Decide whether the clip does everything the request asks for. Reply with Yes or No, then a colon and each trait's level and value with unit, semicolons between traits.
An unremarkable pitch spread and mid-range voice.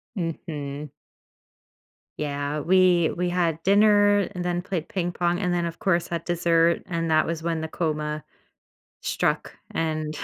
No: narrow, 2.2 semitones; medium, 170 Hz